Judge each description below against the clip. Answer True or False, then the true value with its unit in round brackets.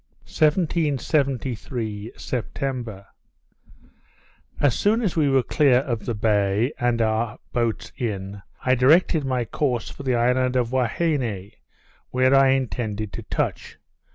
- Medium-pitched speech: False (125 Hz)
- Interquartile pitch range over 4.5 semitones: False (3.5 semitones)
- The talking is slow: True (125 wpm)